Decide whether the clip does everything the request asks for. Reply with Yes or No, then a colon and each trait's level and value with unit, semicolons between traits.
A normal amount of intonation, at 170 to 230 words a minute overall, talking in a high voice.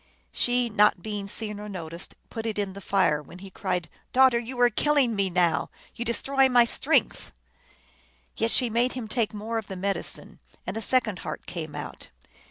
Yes: average, 3.9 semitones; average, 190 wpm; high, 215 Hz